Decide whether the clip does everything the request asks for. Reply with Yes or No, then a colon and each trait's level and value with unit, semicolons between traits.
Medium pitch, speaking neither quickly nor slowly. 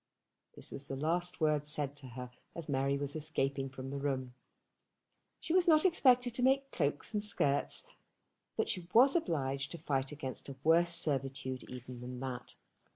Yes: medium, 145 Hz; average, 170 wpm